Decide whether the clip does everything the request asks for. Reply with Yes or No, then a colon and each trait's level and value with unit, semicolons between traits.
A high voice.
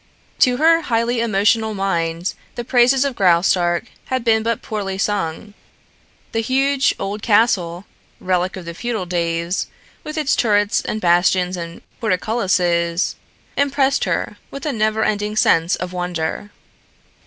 Yes: high, 205 Hz